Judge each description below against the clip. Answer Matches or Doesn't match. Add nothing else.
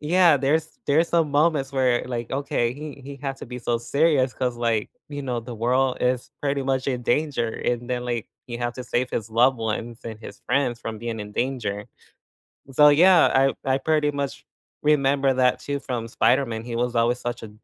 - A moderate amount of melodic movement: Matches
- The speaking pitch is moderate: Doesn't match